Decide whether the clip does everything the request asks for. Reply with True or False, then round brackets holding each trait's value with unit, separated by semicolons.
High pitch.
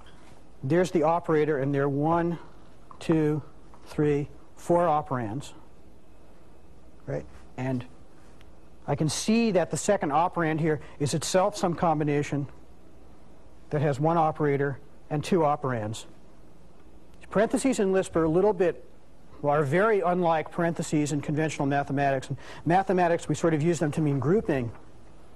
False (150 Hz)